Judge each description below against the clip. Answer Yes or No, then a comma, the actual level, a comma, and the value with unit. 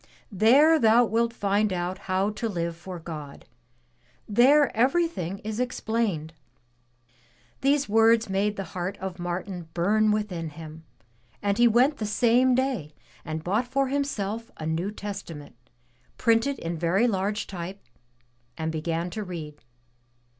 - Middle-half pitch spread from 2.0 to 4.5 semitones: No, average, 5.1 semitones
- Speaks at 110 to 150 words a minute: Yes, slow, 135 wpm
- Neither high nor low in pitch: No, high, 200 Hz